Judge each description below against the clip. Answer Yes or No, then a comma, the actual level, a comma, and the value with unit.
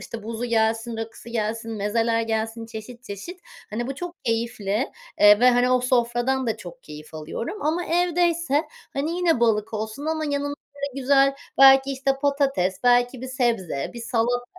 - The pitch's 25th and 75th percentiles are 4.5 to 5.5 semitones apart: No, average, 3.5 semitones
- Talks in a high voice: Yes, high, 240 Hz